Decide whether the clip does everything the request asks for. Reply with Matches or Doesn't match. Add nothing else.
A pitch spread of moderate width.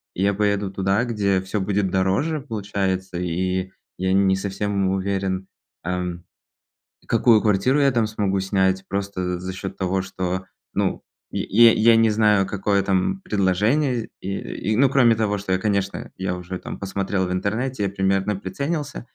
Doesn't match